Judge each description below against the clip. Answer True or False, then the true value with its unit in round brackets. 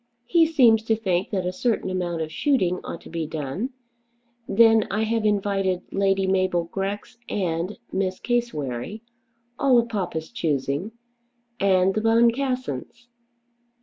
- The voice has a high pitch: True (195 Hz)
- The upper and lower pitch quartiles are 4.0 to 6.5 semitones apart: True (4.4 semitones)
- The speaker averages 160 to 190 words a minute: False (135 wpm)